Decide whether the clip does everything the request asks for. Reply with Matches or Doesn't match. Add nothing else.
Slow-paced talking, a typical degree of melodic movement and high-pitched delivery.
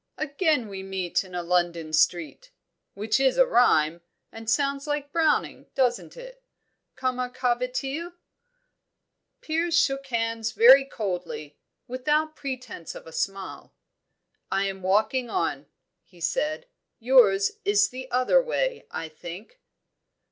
Doesn't match